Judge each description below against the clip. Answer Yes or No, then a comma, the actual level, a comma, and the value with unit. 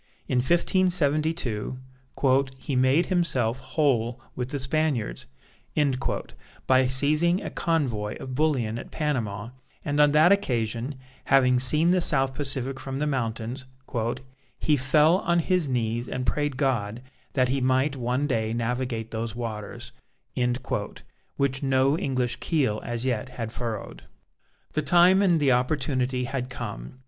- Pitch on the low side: Yes, low, 130 Hz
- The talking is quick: No, slow, 135 wpm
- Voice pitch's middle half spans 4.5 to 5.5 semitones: No, average, 3.7 semitones